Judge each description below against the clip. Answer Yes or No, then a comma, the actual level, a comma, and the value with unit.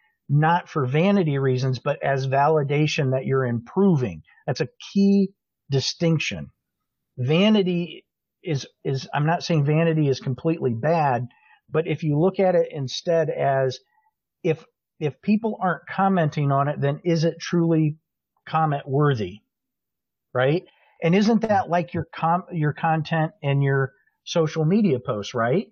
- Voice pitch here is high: No, medium, 160 Hz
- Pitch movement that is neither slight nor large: Yes, average, 4.1 semitones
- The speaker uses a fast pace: No, average, 140 wpm